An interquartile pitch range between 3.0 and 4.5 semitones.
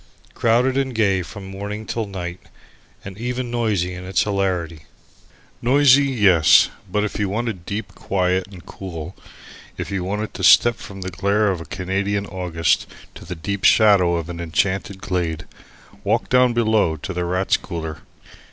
Yes: average, 3.3 semitones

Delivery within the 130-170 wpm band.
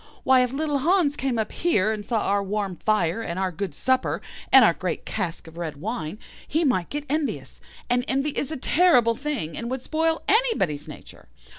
No: average, 200 wpm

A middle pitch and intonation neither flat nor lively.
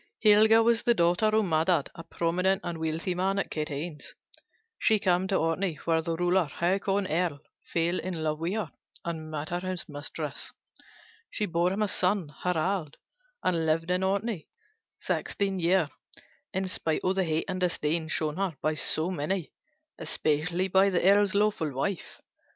Yes: medium, 175 Hz; average, 3.2 semitones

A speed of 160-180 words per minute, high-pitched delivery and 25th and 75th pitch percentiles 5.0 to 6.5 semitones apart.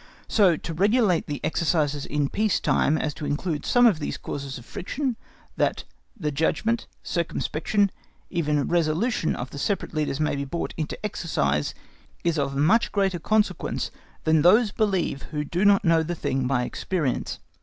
No: average, 165 wpm; medium, 165 Hz; average, 5.3 semitones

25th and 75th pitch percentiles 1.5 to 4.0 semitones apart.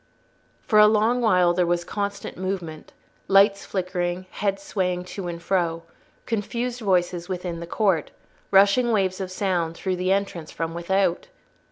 Yes: narrow, 2.4 semitones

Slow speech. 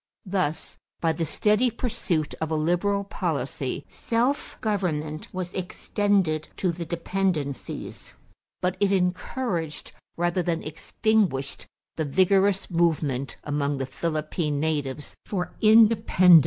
Yes: slow, 115 wpm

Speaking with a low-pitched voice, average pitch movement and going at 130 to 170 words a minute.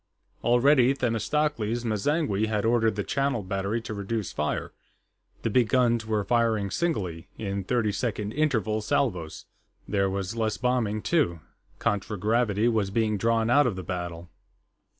Yes: low, 110 Hz; average, 3.4 semitones; average, 140 wpm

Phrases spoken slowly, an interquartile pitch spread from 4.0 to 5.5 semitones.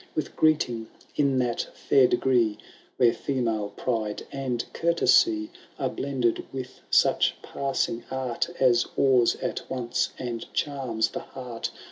No: slow, 125 wpm; narrow, 2.6 semitones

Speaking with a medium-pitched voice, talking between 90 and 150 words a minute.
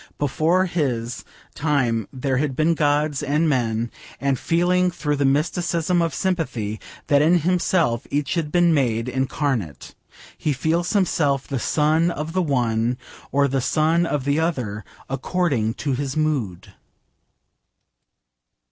Yes: medium, 145 Hz; slow, 135 wpm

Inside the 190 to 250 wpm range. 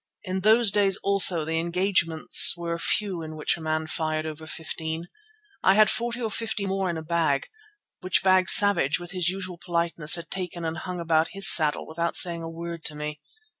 Yes: average, 195 wpm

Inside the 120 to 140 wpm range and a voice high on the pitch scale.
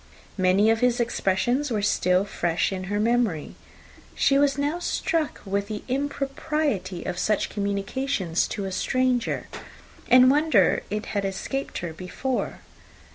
Yes: slow, 135 wpm; high, 215 Hz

